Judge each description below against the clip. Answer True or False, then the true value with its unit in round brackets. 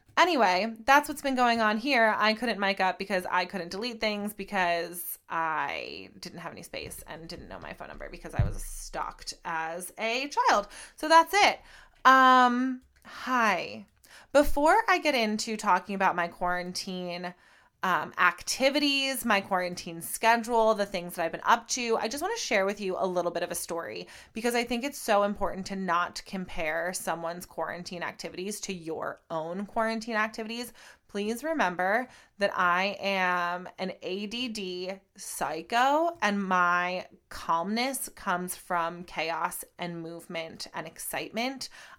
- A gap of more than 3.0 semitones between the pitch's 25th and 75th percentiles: True (4.9 semitones)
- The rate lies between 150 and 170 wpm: True (155 wpm)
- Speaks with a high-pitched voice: True (195 Hz)